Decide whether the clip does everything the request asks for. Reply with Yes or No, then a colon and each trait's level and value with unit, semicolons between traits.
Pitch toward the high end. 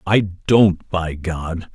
No: very low, 90 Hz